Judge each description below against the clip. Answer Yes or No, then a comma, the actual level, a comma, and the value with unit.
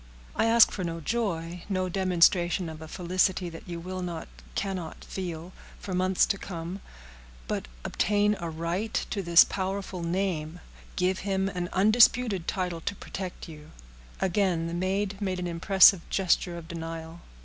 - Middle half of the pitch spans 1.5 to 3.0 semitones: Yes, narrow, 2.5 semitones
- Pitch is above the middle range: No, medium, 180 Hz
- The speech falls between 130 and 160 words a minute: Yes, average, 150 wpm